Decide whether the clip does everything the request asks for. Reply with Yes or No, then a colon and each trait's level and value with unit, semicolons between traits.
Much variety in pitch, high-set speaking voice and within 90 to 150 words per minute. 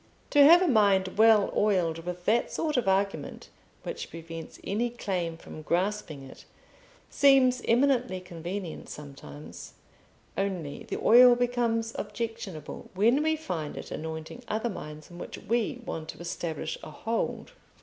Yes: wide, 6.4 semitones; high, 200 Hz; average, 140 wpm